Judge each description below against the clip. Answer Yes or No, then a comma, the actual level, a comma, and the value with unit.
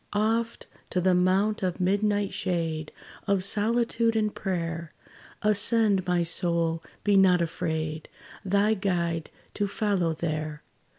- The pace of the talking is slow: Yes, slow, 120 wpm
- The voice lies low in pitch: No, medium, 185 Hz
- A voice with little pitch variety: No, average, 3.6 semitones